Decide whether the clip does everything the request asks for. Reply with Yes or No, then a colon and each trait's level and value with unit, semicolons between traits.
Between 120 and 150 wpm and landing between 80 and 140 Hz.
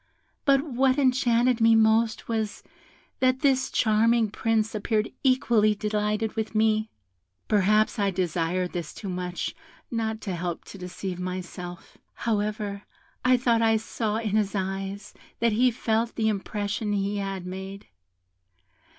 No: slow, 135 wpm; high, 215 Hz